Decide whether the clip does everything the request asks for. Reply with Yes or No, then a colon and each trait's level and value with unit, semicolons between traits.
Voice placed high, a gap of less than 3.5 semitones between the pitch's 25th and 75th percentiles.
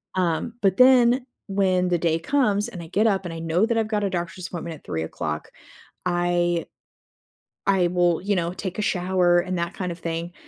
No: medium, 180 Hz; average, 2.7 semitones